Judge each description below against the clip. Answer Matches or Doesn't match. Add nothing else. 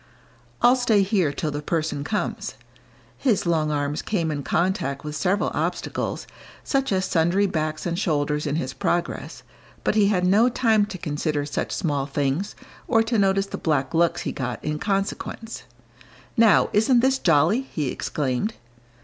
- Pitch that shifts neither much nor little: Doesn't match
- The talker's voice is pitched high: Doesn't match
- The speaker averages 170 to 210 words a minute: Doesn't match